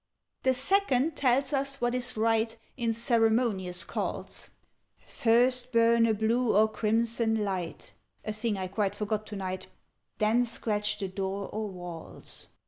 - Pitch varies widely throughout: No, average, 2.9 semitones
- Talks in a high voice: Yes, high, 225 Hz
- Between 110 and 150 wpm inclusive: Yes, average, 140 wpm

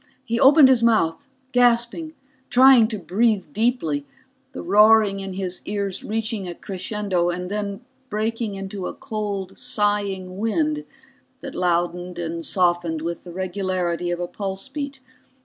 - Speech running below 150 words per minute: Yes, average, 140 wpm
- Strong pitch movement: No, average, 4.1 semitones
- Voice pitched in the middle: No, high, 200 Hz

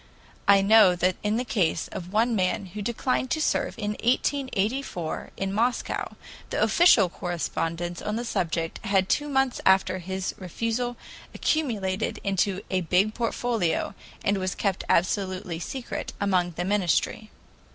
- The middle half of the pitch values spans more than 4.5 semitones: No, average, 4.0 semitones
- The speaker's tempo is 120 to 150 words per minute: Yes, average, 140 wpm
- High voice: Yes, high, 200 Hz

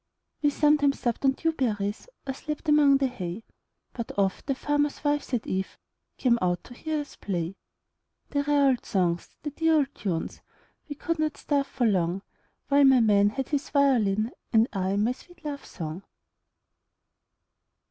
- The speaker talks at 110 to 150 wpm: Yes, average, 145 wpm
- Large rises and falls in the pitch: Yes, wide, 6.4 semitones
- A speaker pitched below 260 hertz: No, very high, 265 Hz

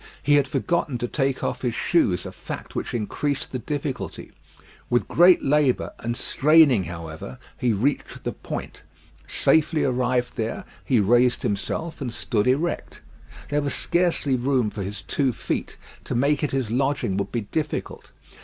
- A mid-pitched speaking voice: No, low, 130 Hz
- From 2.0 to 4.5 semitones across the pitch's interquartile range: Yes, average, 4.0 semitones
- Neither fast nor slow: Yes, average, 160 wpm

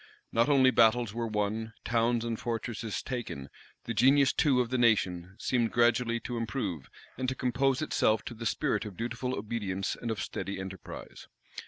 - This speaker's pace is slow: No, average, 170 wpm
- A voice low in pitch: Yes, low, 115 Hz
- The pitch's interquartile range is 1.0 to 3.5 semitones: Yes, average, 2.7 semitones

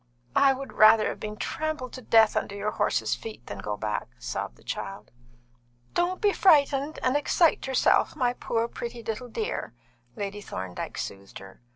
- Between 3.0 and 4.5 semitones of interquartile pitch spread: No, wide, 5.5 semitones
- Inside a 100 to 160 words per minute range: No, average, 170 wpm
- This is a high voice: Yes, high, 225 Hz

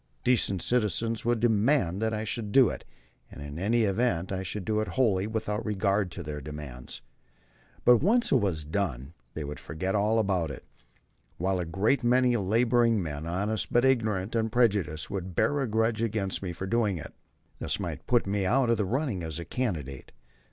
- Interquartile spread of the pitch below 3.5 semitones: No, average, 4.8 semitones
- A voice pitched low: Yes, low, 105 Hz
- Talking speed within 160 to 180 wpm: No, average, 190 wpm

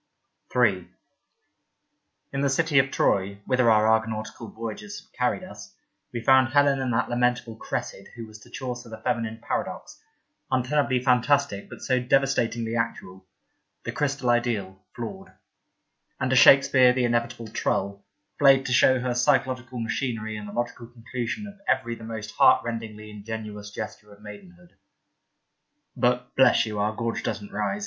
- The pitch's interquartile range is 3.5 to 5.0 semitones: No, average, 3.1 semitones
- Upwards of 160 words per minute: No, average, 155 wpm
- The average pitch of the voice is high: No, low, 120 Hz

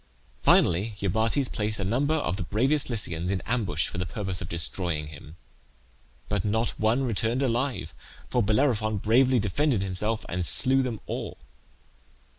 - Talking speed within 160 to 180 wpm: No, average, 150 wpm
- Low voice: Yes, low, 110 Hz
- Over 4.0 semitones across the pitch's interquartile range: Yes, average, 5.1 semitones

